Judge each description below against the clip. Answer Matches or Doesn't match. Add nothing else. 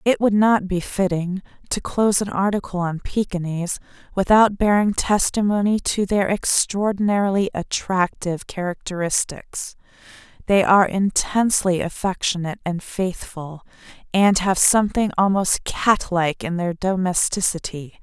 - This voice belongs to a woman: Matches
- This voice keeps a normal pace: Doesn't match